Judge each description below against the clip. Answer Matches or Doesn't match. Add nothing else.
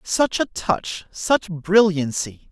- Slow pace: Matches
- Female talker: Doesn't match